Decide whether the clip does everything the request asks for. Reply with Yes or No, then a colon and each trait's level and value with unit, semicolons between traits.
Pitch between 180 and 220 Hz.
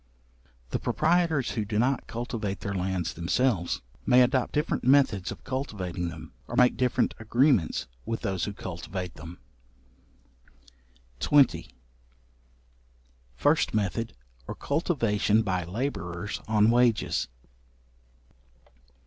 No: low, 110 Hz